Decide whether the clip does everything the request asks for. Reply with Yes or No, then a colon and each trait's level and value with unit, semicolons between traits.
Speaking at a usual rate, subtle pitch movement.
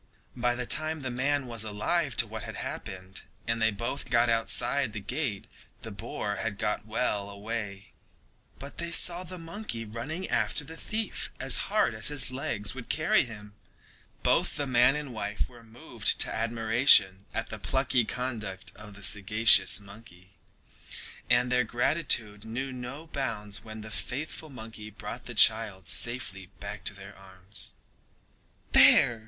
No: average, 160 wpm; average, 4.1 semitones